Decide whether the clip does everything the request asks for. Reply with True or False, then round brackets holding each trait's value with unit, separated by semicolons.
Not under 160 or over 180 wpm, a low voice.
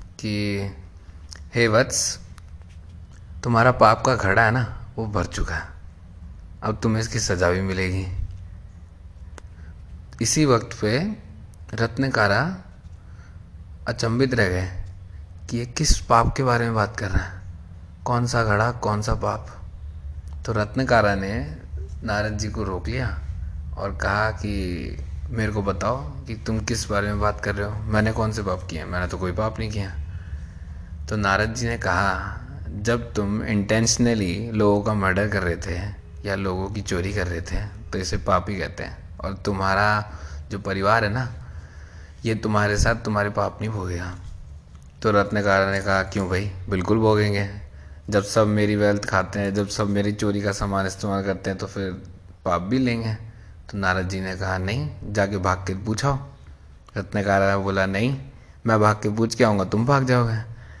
True (165 wpm; 100 Hz)